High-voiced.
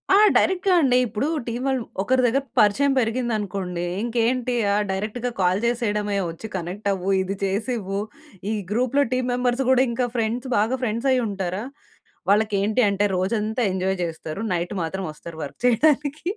Yes: high, 220 Hz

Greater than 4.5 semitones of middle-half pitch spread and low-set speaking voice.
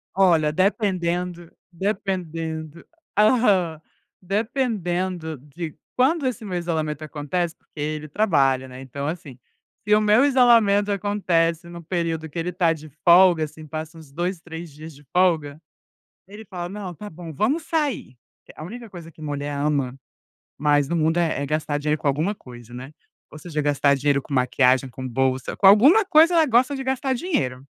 No: average, 5.3 semitones; medium, 170 Hz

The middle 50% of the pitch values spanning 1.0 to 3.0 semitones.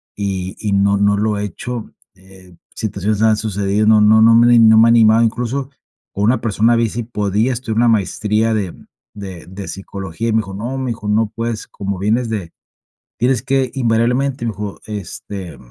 Yes: narrow, 2.6 semitones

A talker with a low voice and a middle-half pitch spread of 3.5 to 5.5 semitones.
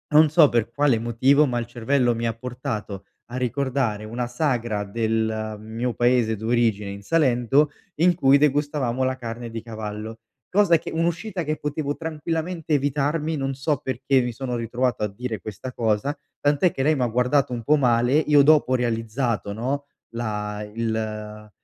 Yes: low, 125 Hz; average, 4.2 semitones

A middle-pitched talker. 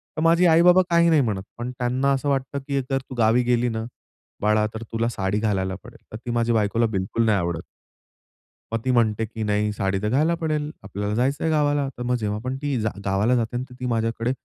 No: low, 120 Hz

